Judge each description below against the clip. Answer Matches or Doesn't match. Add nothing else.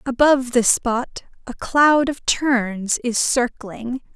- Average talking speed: Doesn't match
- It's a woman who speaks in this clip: Matches